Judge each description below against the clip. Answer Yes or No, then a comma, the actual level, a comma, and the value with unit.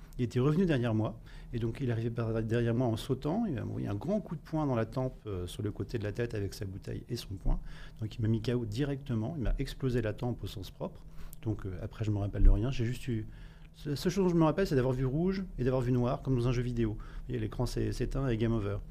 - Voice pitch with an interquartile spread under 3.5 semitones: No, average, 3.8 semitones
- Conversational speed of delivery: No, fast, 290 wpm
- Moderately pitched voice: No, low, 120 Hz